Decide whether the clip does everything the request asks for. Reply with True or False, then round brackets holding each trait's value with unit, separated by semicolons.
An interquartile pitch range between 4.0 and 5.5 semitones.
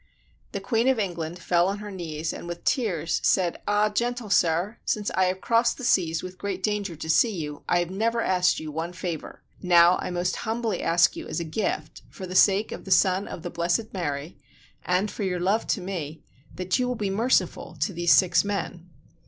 False (3.4 semitones)